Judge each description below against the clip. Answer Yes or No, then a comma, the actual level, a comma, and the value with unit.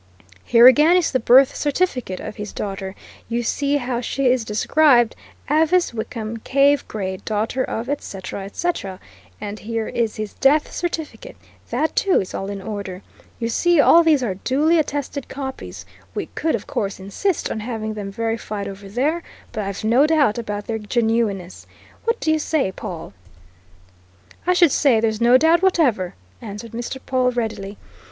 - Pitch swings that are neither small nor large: No, wide, 5.7 semitones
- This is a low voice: No, high, 235 Hz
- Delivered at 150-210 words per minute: Yes, average, 170 wpm